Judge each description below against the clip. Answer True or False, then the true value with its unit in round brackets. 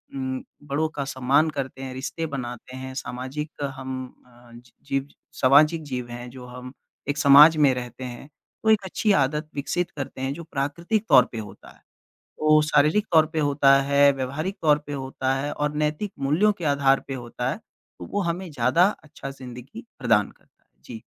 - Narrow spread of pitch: False (3.1 semitones)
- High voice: False (140 Hz)